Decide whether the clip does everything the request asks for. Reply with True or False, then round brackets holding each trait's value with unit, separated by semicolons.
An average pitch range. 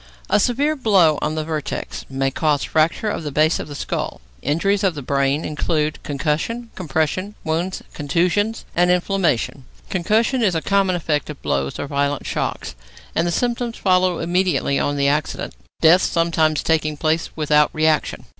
True (3.9 semitones)